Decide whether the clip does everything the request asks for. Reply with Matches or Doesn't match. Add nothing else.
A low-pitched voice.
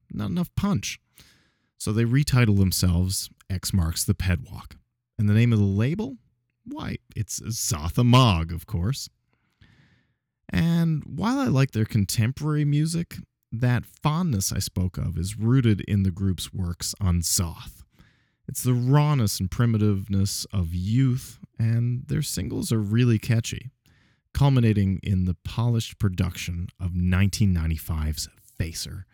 Matches